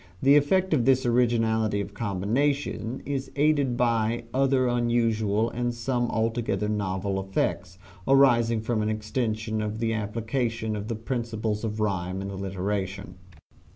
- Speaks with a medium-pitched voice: No, low, 115 Hz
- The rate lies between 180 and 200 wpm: No, slow, 135 wpm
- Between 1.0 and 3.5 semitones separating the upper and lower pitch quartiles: Yes, narrow, 2.6 semitones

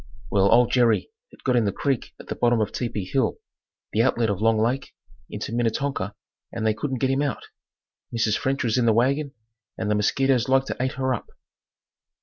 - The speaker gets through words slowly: No, average, 200 wpm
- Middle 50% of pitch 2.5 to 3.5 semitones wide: Yes, average, 3.2 semitones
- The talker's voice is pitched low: Yes, low, 120 Hz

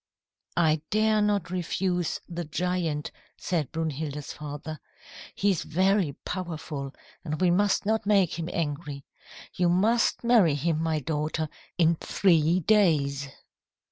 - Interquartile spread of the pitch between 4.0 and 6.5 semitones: No, average, 3.6 semitones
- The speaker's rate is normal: No, slow, 125 wpm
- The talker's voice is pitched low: No, medium, 170 Hz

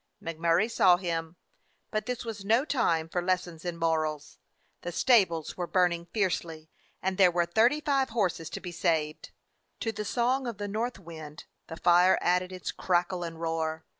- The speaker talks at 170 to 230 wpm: Yes, average, 175 wpm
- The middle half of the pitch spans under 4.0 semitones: No, average, 4.3 semitones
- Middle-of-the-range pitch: Yes, medium, 175 Hz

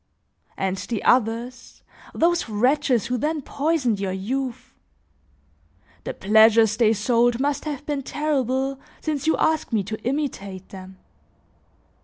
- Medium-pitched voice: No, high, 245 Hz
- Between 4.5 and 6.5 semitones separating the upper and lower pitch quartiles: Yes, average, 4.9 semitones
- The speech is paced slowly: Yes, slow, 125 wpm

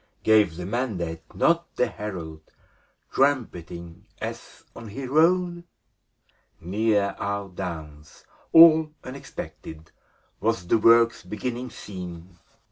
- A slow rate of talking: Yes, slow, 100 wpm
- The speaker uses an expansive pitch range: Yes, wide, 6.6 semitones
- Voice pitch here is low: Yes, low, 105 Hz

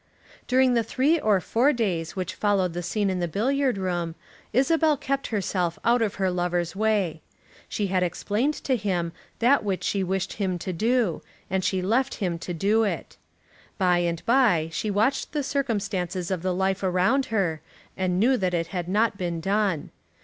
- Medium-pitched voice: No, high, 195 Hz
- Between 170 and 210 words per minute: Yes, average, 180 wpm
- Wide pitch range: No, average, 4.5 semitones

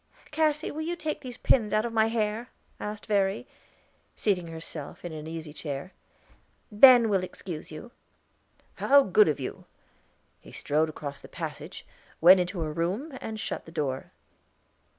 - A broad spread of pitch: Yes, wide, 6.4 semitones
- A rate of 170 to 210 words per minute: No, average, 160 wpm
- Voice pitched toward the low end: No, high, 195 Hz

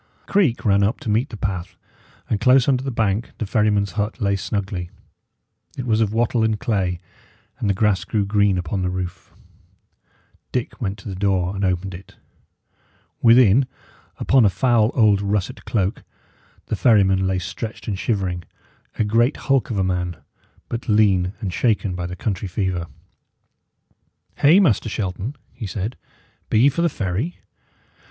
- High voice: No, low, 105 Hz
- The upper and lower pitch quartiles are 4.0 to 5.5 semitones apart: No, average, 3.3 semitones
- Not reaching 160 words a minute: No, average, 165 wpm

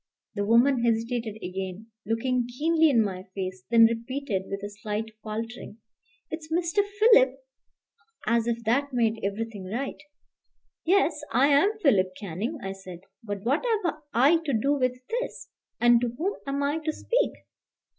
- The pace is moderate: Yes, average, 155 wpm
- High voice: Yes, high, 235 Hz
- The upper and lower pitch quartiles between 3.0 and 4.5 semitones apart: No, average, 5.1 semitones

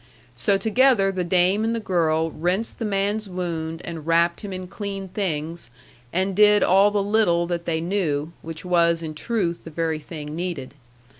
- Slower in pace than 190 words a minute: Yes, average, 175 wpm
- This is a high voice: No, medium, 175 Hz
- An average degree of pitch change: Yes, average, 3.3 semitones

